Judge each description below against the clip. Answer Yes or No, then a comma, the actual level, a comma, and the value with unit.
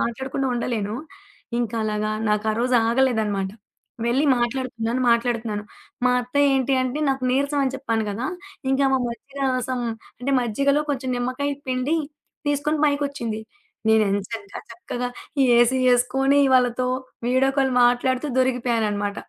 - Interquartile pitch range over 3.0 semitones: No, average, 2.7 semitones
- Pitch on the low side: No, very high, 250 Hz